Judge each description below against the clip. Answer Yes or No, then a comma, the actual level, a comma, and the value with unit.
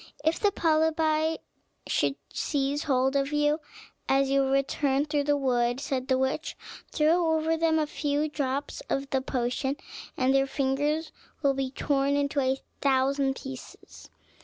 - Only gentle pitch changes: Yes, narrow, 2.2 semitones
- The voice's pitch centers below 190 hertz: No, very high, 280 Hz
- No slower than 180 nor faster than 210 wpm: No, average, 150 wpm